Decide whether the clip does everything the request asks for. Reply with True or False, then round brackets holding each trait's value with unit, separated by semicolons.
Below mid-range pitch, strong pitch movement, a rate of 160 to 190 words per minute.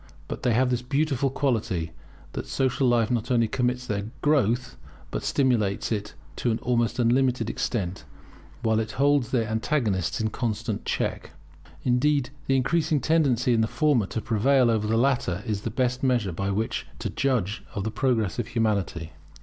False (120 Hz; 3.3 semitones; 170 wpm)